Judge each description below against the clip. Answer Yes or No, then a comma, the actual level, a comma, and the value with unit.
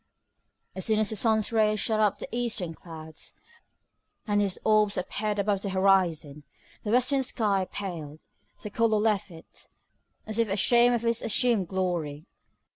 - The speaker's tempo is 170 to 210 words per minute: No, average, 160 wpm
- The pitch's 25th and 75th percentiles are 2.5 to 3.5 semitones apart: Yes, average, 3.1 semitones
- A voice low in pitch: No, high, 205 Hz